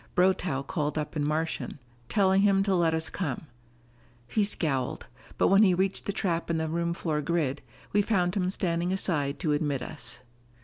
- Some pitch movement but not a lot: Yes, average, 4.0 semitones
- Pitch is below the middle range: No, medium, 170 Hz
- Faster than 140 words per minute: Yes, average, 180 wpm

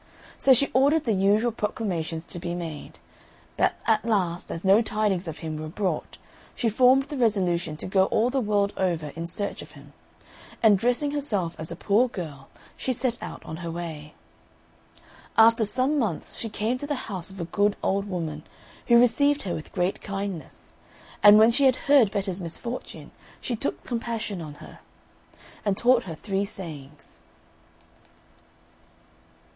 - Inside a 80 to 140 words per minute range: No, average, 165 wpm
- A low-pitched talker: No, high, 200 Hz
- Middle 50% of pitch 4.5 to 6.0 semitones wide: Yes, wide, 5.5 semitones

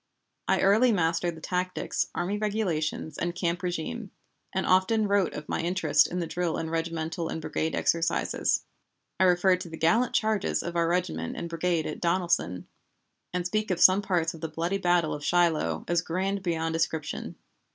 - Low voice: No, medium, 175 Hz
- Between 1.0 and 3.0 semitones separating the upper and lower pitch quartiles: Yes, narrow, 2.5 semitones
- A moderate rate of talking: Yes, average, 175 wpm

